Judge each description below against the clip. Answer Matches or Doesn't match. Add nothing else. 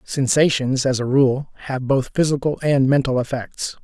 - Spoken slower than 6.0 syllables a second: Matches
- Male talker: Matches